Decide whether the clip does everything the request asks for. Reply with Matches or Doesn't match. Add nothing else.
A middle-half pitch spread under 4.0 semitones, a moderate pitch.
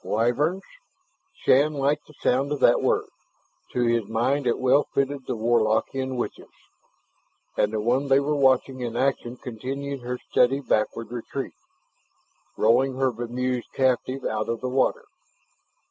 Doesn't match